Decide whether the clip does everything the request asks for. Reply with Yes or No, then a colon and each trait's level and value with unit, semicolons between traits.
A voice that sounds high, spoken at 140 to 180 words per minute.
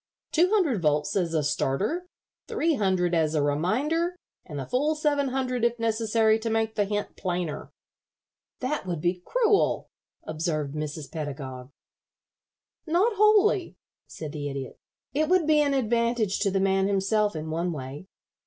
Yes: high, 205 Hz; average, 155 wpm